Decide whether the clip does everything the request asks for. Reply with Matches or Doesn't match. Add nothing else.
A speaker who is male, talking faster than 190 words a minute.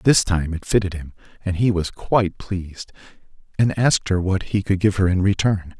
Matches